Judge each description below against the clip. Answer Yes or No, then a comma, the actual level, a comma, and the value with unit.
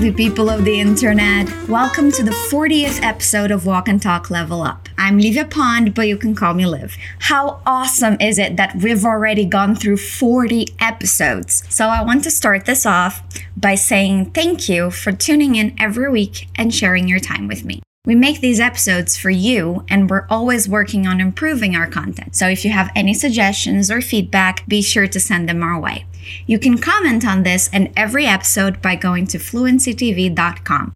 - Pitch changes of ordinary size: Yes, average, 4.0 semitones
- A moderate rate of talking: No, fast, 190 wpm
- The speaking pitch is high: Yes, high, 205 Hz